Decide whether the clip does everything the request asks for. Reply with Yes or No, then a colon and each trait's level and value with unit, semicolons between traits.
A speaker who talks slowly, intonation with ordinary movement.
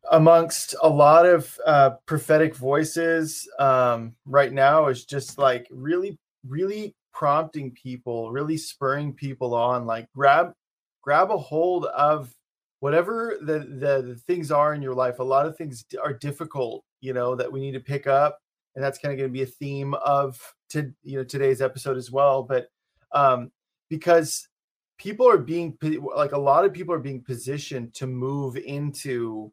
No: average, 170 wpm; average, 3.1 semitones